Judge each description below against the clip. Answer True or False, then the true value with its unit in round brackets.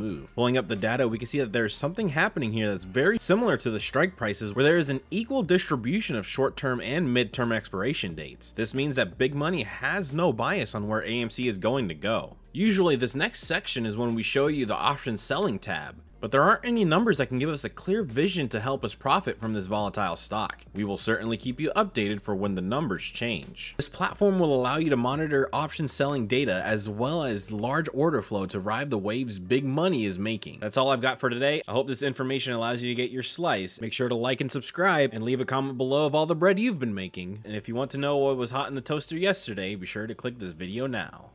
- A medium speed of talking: False (250 wpm)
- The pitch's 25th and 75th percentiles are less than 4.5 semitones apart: False (5.3 semitones)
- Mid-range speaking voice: False (130 Hz)